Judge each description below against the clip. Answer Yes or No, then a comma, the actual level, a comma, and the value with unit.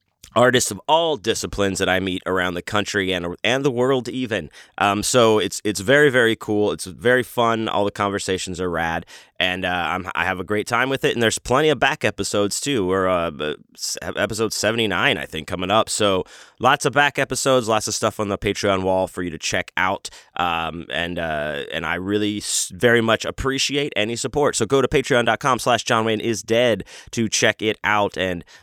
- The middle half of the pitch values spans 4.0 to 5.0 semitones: Yes, average, 4.7 semitones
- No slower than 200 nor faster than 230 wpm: Yes, fast, 205 wpm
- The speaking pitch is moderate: No, low, 105 Hz